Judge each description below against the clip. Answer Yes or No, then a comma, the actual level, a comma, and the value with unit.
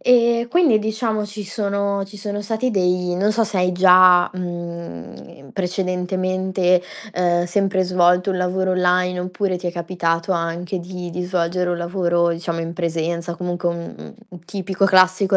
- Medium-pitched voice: Yes, medium, 180 Hz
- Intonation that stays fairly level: Yes, narrow, 2.0 semitones